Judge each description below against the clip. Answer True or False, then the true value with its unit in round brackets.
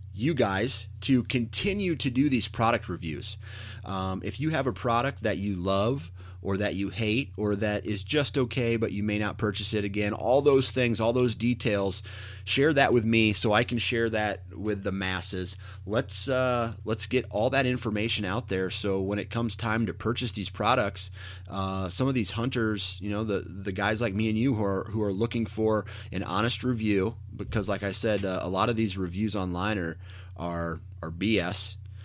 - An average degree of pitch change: True (3.1 semitones)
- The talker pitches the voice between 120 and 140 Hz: False (105 Hz)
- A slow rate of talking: False (200 wpm)